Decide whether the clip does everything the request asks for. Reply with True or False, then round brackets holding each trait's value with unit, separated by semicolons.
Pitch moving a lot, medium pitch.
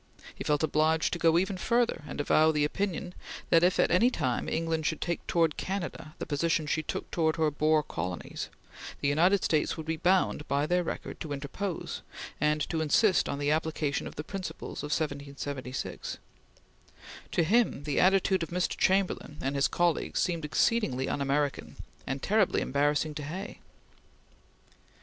False (3.4 semitones; 160 Hz)